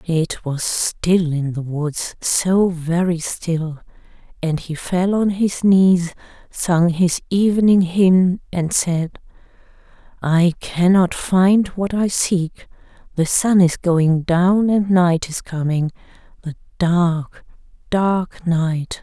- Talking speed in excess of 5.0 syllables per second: No, 3.0 syllables/s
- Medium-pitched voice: Yes, medium, 175 Hz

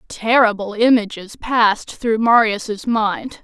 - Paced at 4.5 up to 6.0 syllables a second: No, 3.7 syllables/s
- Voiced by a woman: Yes, female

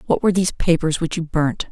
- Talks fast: Yes, fast, 245 wpm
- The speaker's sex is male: No, female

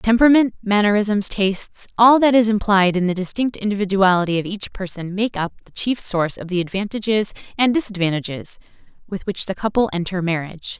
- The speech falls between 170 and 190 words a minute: No, average, 155 wpm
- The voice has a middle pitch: No, high, 200 Hz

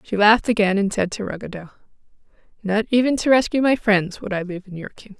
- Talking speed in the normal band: No, fast, 220 wpm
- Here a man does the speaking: No, female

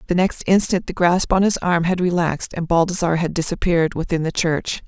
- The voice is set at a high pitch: No, medium, 175 Hz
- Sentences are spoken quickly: Yes, fast, 220 wpm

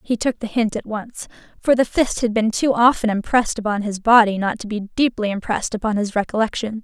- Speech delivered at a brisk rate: Yes, fast, 220 wpm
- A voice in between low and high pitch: No, high, 220 Hz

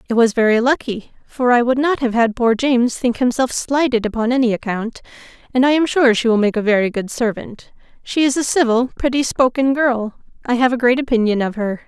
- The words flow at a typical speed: No, fast, 215 wpm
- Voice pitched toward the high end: Yes, high, 240 Hz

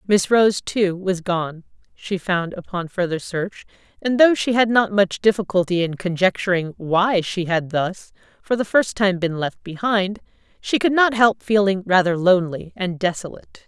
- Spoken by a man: No, female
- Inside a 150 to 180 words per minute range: Yes, average, 170 wpm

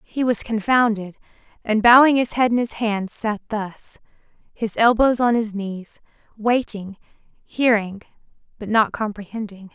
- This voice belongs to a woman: Yes, female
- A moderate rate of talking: No, slow, 125 wpm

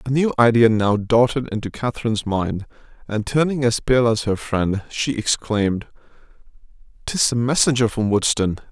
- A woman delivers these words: No, male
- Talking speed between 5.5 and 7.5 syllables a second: No, 5.0 syllables/s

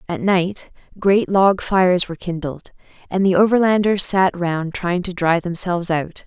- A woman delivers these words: Yes, female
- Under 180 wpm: Yes, average, 165 wpm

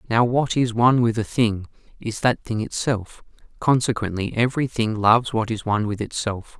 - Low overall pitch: Yes, low, 115 Hz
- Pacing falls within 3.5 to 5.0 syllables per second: No, 5.3 syllables/s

